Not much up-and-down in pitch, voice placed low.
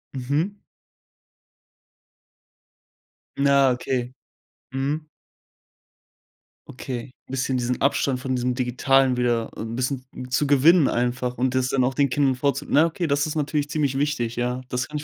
Yes: narrow, 2.3 semitones; low, 130 Hz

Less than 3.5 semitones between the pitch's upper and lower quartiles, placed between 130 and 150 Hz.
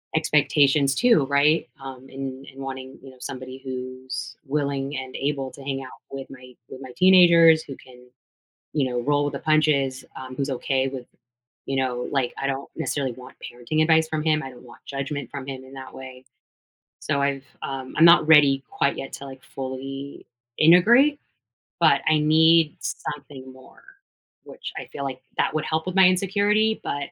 Yes: average, 2.8 semitones; low, 135 Hz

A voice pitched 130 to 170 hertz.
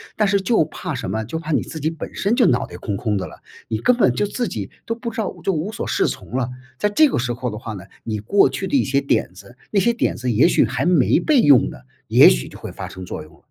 Yes: medium, 140 Hz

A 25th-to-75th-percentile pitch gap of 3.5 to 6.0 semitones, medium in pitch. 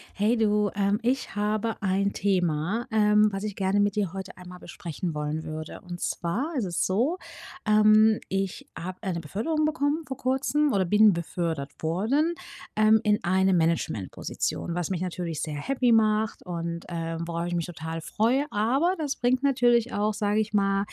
No: average, 4.3 semitones; high, 205 Hz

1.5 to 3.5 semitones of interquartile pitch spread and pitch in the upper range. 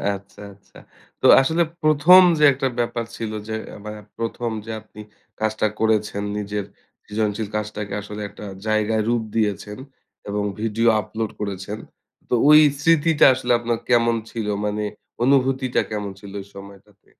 No: narrow, 2.5 semitones; low, 110 Hz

